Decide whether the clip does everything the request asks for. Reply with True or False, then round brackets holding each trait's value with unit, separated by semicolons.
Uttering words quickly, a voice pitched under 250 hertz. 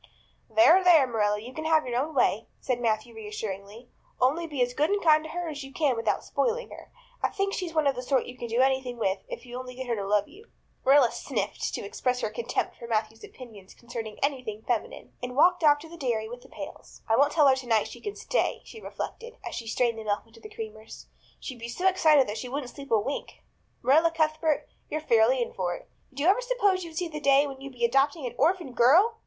False (245 wpm; 260 Hz)